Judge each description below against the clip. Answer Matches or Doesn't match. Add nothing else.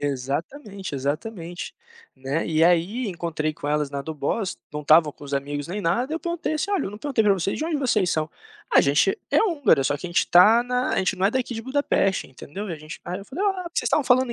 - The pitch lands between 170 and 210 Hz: Matches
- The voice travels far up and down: Matches